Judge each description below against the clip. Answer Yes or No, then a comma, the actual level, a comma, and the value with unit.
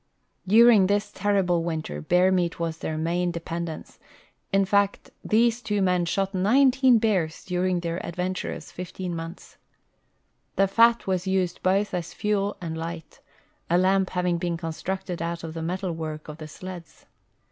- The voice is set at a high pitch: No, medium, 180 Hz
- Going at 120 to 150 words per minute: No, average, 160 wpm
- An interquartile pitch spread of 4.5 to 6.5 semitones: No, average, 2.7 semitones